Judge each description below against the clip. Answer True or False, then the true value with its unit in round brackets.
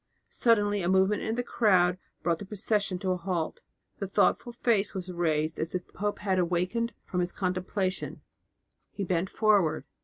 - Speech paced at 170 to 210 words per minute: True (175 wpm)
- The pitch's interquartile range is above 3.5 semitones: False (2.6 semitones)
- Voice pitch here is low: False (190 Hz)